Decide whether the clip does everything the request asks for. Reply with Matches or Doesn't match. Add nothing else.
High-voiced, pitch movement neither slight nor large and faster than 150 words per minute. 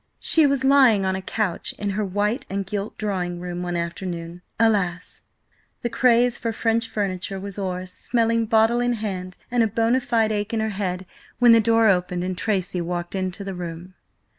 Matches